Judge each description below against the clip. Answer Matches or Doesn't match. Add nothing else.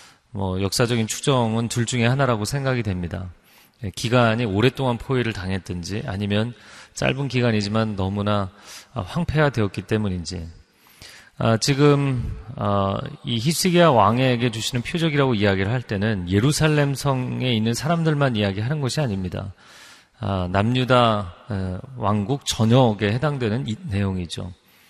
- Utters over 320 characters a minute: Doesn't match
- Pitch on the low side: Matches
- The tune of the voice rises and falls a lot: Doesn't match